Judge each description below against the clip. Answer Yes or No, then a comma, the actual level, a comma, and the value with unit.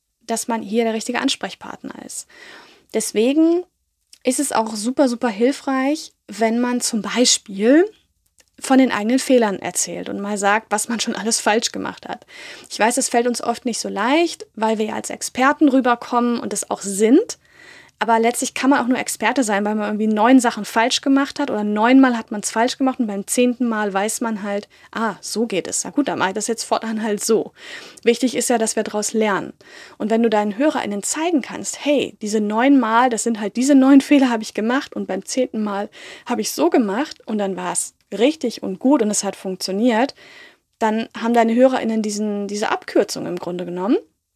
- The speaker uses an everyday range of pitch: Yes, average, 3.5 semitones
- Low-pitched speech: No, high, 230 Hz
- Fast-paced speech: Yes, fast, 205 wpm